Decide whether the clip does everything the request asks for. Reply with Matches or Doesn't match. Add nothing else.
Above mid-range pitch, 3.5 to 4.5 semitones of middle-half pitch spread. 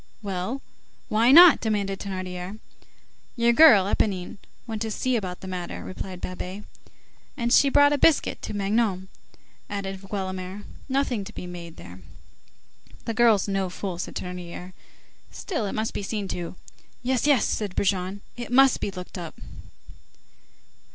Matches